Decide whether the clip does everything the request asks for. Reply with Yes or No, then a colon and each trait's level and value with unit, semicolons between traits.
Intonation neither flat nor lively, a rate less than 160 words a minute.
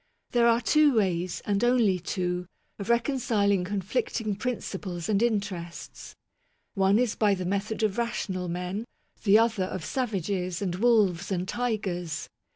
Yes: average, 4.0 semitones; average, 140 wpm